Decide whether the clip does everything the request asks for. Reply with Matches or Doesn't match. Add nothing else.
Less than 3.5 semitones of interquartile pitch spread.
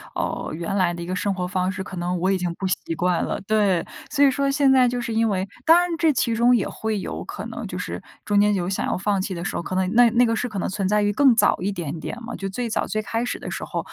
Doesn't match